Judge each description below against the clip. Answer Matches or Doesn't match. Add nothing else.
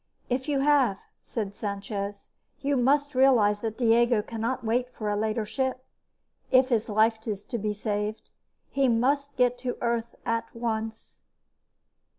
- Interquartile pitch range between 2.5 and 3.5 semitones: Matches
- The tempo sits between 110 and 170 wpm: Matches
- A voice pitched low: Doesn't match